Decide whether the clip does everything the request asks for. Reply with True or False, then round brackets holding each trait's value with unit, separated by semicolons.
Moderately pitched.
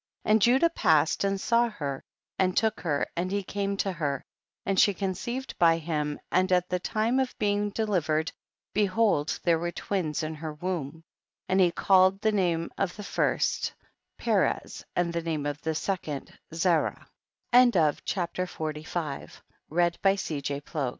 True (180 Hz)